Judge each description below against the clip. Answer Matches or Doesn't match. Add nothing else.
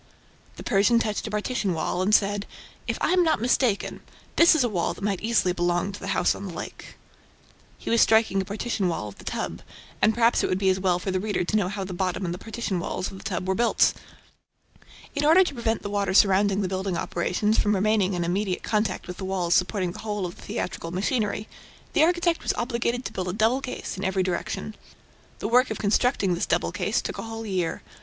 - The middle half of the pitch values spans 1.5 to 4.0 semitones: Matches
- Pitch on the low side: Doesn't match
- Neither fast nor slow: Doesn't match